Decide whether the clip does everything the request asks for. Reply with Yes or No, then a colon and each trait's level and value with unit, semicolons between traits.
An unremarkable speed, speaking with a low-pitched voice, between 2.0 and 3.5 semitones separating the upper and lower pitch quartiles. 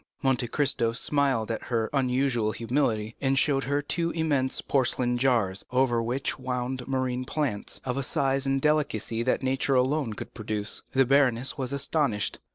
Yes: average, 160 wpm; low, 130 Hz; average, 2.7 semitones